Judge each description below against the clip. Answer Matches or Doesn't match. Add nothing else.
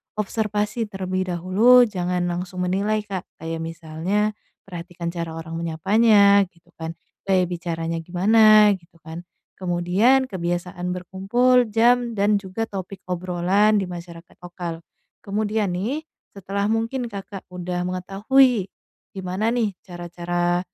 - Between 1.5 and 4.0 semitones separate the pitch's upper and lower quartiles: Matches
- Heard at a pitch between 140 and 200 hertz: Matches